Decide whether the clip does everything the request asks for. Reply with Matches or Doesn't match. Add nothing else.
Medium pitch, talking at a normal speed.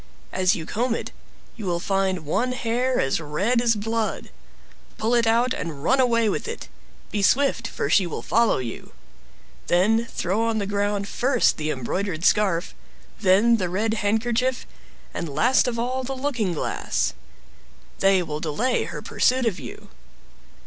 Doesn't match